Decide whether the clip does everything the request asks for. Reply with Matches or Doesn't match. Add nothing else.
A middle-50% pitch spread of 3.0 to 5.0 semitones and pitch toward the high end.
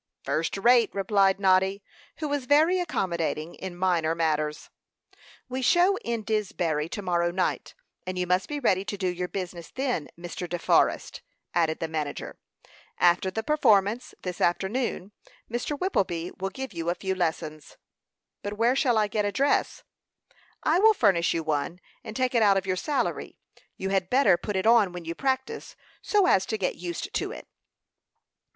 Doesn't match